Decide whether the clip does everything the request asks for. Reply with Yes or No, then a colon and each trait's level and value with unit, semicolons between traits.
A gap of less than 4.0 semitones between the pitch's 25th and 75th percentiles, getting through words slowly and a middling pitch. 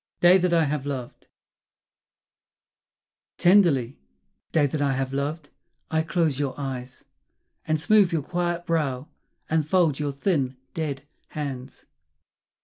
Yes: average, 3.6 semitones; slow, 125 wpm; medium, 150 Hz